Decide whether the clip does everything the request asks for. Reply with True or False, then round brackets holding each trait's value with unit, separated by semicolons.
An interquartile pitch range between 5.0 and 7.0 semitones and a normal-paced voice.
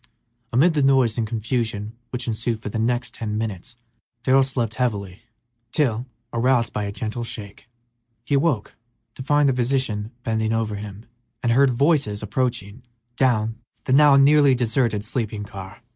False (3.5 semitones; 155 wpm)